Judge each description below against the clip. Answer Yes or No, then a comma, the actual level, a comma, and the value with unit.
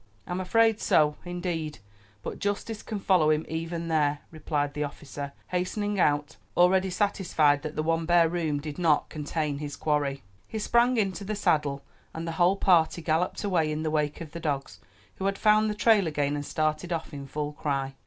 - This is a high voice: No, medium, 160 Hz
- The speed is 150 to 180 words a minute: No, average, 190 wpm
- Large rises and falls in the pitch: No, average, 3.9 semitones